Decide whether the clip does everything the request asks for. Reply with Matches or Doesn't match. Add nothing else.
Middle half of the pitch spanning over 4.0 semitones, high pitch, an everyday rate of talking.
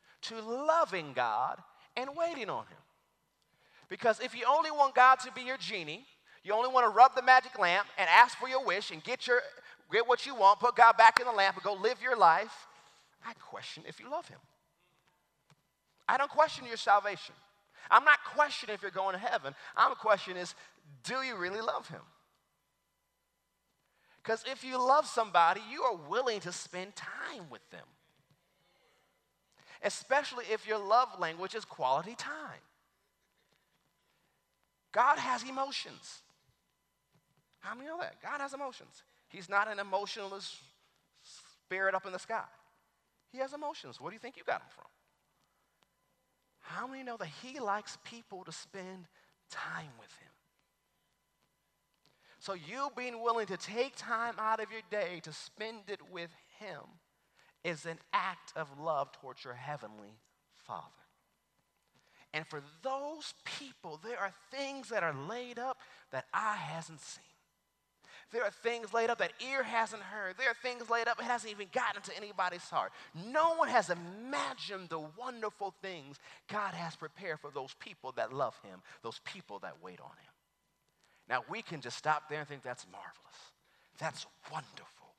Matches